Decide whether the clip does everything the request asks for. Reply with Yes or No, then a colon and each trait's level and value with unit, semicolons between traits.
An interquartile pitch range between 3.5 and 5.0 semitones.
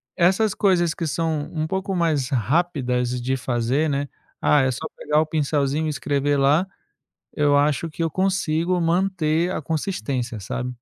Yes: average, 3.9 semitones